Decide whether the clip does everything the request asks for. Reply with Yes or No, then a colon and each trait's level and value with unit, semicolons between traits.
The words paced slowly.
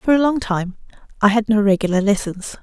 No: fast, 205 wpm